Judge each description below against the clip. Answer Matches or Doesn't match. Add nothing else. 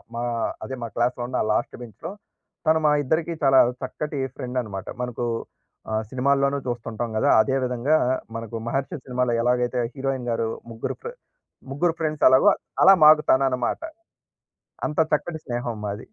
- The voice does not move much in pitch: Doesn't match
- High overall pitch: Doesn't match